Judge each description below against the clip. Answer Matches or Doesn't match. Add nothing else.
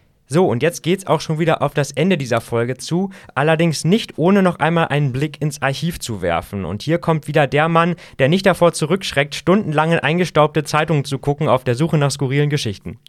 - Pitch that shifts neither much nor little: Matches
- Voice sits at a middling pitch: Matches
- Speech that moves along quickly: Matches